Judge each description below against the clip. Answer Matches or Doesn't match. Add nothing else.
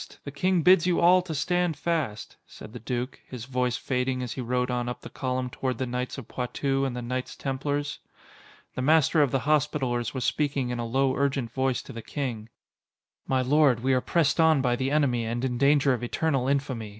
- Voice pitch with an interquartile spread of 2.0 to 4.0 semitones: Matches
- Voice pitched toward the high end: Doesn't match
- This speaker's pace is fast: Matches